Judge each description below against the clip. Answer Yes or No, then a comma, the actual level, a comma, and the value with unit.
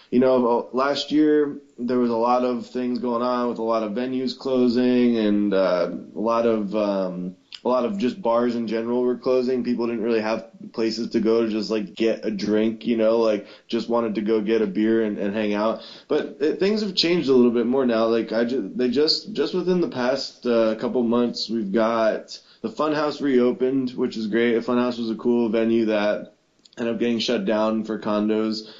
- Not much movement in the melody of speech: Yes, narrow, 2.0 semitones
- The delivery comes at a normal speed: No, fast, 215 wpm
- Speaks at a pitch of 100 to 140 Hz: Yes, low, 115 Hz